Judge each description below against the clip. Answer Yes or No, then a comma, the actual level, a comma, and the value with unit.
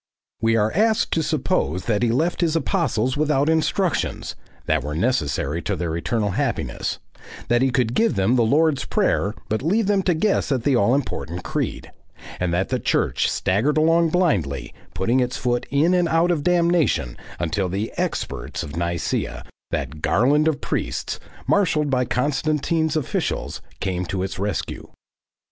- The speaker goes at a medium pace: Yes, average, 160 wpm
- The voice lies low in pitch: Yes, low, 130 Hz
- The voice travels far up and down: Yes, wide, 8.7 semitones